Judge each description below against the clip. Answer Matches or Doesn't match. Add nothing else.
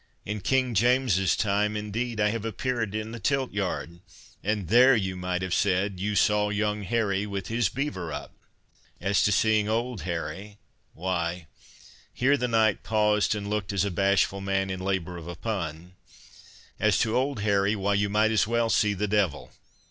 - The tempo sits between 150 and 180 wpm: Matches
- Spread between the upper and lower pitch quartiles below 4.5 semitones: Matches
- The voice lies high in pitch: Doesn't match